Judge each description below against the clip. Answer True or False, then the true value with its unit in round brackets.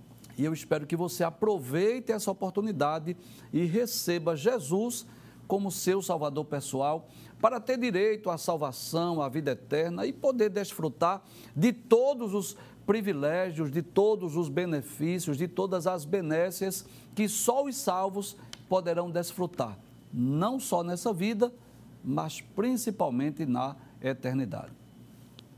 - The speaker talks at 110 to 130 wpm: True (120 wpm)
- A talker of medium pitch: True (180 Hz)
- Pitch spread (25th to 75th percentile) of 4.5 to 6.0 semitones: True (5.0 semitones)